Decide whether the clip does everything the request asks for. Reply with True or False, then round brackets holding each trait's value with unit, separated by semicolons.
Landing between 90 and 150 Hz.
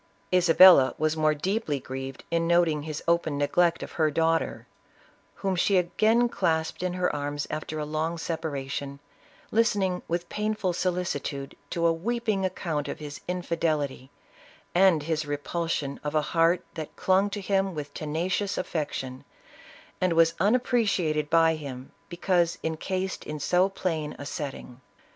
False (165 Hz)